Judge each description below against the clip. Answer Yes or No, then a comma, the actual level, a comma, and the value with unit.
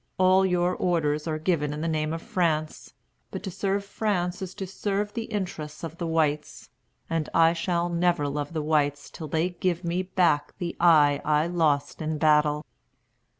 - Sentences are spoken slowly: No, average, 180 wpm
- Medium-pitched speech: Yes, medium, 165 Hz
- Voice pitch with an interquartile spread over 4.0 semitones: No, average, 3.1 semitones